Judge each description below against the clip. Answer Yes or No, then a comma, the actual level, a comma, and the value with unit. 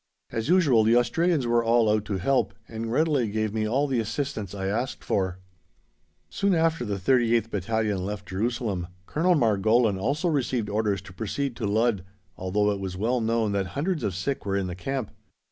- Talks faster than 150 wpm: Yes, average, 185 wpm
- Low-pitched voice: Yes, low, 110 Hz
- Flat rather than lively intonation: No, average, 4.3 semitones